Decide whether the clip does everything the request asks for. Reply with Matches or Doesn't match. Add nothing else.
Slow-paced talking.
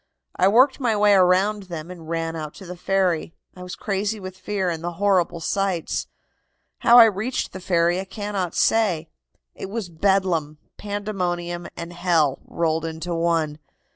Doesn't match